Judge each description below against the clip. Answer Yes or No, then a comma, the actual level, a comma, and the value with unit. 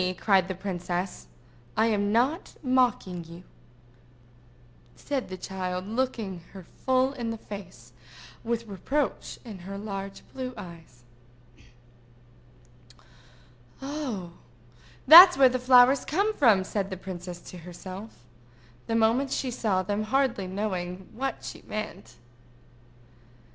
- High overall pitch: Yes, high, 205 Hz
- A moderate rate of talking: No, slow, 115 wpm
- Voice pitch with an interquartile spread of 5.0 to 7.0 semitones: Yes, wide, 5.4 semitones